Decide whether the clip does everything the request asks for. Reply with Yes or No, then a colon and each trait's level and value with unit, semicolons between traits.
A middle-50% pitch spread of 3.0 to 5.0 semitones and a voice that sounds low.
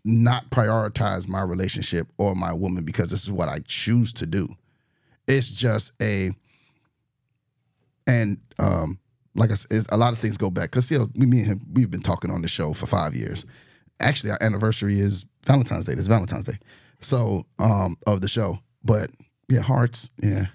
Yes: average, 4.3 semitones; low, 110 Hz